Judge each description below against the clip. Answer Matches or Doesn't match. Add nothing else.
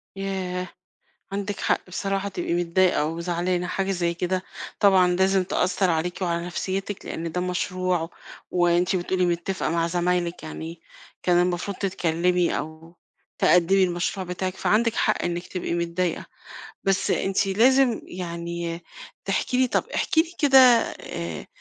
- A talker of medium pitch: Matches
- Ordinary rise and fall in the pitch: Doesn't match